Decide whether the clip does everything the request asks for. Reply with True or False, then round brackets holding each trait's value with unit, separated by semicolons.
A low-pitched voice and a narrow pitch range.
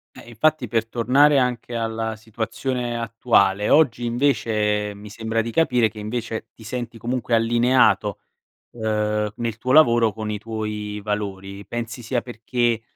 True (115 Hz; 2.1 semitones)